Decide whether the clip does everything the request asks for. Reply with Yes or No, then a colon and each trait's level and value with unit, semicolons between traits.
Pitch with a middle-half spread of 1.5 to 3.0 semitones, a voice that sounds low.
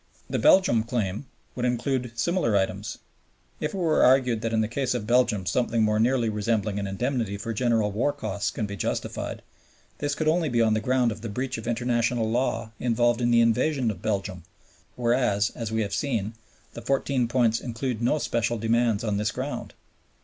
Yes: narrow, 2.6 semitones; low, 115 Hz